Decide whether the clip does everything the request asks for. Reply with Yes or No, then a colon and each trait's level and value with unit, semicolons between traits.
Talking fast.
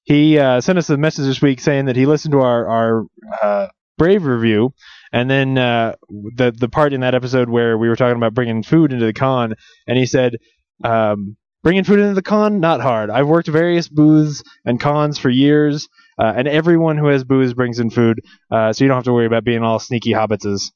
Yes: fast, 225 wpm